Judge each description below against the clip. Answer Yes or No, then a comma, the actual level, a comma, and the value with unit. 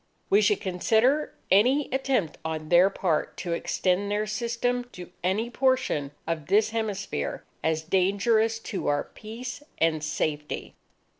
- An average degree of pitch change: No, wide, 5.8 semitones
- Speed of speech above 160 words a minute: No, average, 140 wpm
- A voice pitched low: No, high, 200 Hz